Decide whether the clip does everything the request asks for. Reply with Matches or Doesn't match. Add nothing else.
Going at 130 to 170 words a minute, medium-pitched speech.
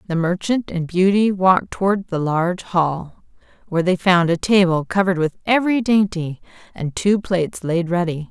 Matches